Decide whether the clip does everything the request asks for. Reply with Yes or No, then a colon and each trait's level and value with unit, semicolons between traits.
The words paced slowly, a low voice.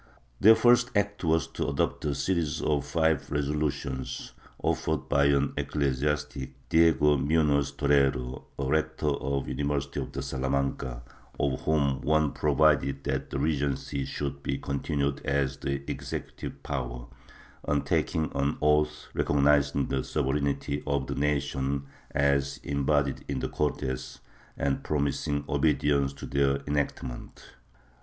Yes: slow, 125 wpm; very low, 70 Hz